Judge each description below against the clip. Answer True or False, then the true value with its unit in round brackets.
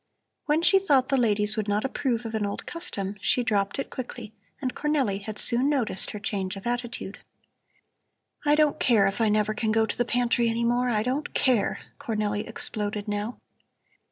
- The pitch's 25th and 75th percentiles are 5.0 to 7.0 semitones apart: False (3.6 semitones)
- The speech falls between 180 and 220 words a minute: True (185 wpm)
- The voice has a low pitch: False (230 Hz)